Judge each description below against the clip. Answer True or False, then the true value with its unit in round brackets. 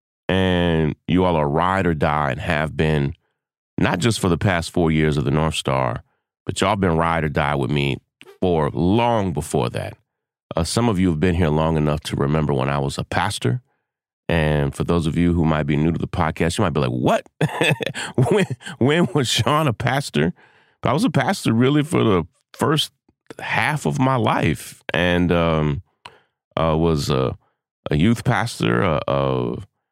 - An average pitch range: True (4.2 semitones)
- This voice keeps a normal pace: True (190 wpm)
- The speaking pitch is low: True (85 Hz)